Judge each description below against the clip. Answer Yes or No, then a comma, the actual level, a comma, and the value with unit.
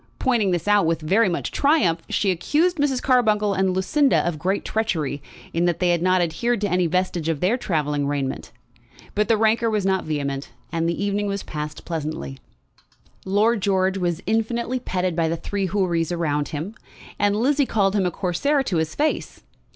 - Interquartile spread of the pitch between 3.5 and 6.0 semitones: Yes, average, 4.7 semitones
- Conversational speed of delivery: Yes, average, 180 wpm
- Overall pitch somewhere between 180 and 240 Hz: Yes, high, 190 Hz